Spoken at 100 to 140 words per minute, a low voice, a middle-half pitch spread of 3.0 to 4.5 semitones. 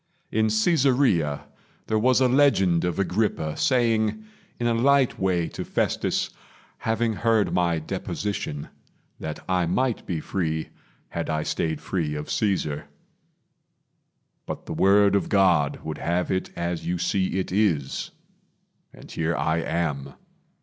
No: slow, 135 wpm; very low, 95 Hz; wide, 5.4 semitones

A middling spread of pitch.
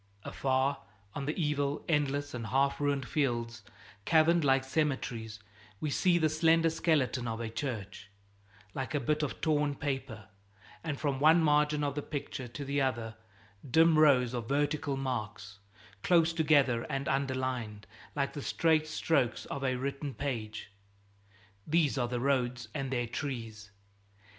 Yes: average, 3.4 semitones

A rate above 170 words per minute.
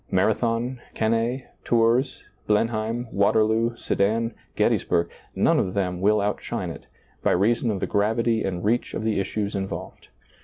No: average, 145 wpm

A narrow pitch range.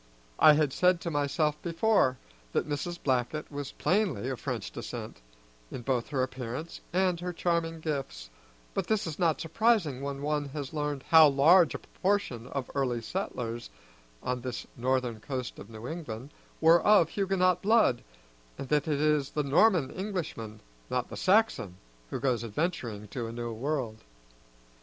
No: average, 5.2 semitones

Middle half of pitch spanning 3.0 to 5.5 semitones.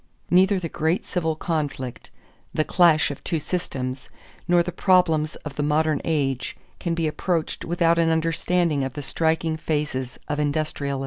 No: narrow, 2.4 semitones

